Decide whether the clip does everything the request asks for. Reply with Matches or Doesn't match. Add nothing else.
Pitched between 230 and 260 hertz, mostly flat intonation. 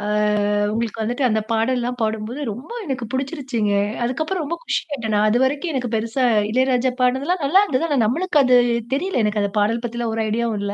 Doesn't match